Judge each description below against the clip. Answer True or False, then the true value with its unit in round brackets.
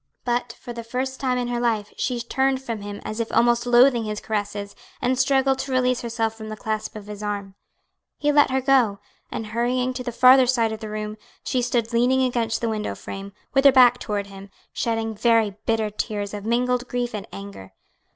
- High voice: True (235 Hz)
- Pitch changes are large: False (2.9 semitones)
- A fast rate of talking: True (210 wpm)